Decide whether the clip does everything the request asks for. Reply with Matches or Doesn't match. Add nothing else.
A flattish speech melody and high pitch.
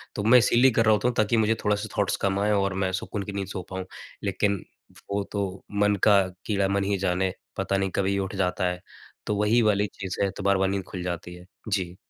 Doesn't match